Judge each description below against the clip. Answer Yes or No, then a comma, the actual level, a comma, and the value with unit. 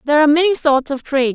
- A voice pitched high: Yes, very high, 295 Hz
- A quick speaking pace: Yes, fast, 265 wpm